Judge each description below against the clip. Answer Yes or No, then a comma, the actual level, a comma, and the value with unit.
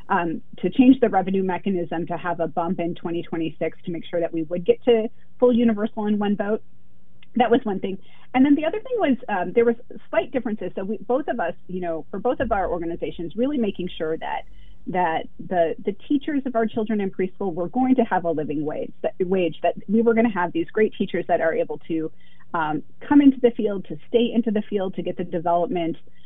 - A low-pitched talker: No, high, 195 Hz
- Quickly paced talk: Yes, fast, 230 wpm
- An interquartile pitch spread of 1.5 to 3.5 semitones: No, wide, 5.5 semitones